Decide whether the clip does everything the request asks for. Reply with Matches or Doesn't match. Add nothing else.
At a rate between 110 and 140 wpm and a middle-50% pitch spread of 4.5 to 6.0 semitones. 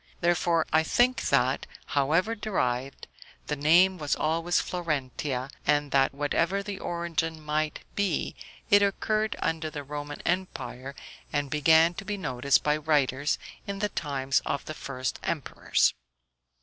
Doesn't match